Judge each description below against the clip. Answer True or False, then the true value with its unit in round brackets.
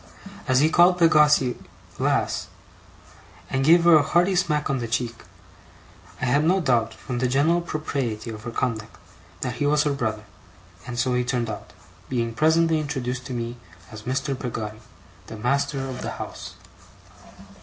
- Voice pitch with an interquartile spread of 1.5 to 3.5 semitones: False (4.2 semitones)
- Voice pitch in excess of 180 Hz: False (130 Hz)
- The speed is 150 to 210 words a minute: True (165 wpm)